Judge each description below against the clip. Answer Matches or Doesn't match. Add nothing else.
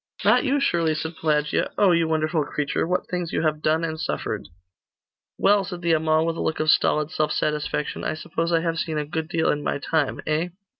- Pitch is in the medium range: Matches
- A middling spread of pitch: Doesn't match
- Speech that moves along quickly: Matches